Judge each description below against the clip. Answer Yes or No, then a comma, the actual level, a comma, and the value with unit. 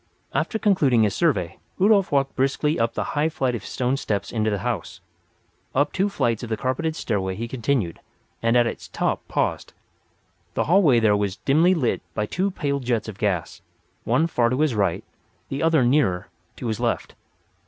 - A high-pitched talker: No, low, 125 Hz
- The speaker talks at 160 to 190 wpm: Yes, average, 180 wpm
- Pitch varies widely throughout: Yes, wide, 5.8 semitones